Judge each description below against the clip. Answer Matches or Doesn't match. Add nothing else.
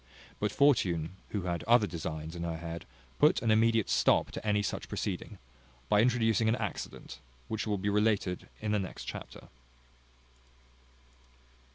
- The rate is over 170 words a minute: Doesn't match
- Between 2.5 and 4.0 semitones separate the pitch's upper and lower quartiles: Doesn't match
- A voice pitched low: Matches